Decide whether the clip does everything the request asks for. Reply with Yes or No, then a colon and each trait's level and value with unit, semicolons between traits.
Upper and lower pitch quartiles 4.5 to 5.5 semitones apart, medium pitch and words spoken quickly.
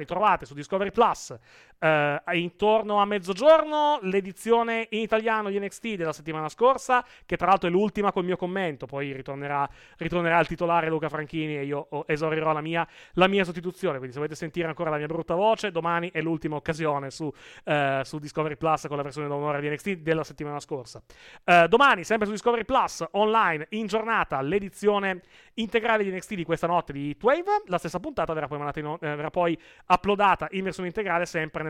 Yes: average, 4.9 semitones; medium, 170 Hz; fast, 190 wpm